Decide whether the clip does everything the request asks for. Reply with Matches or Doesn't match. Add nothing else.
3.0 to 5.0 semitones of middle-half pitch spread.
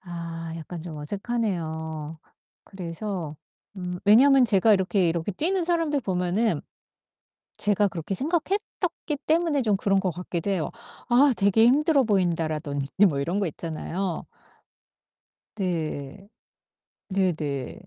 Doesn't match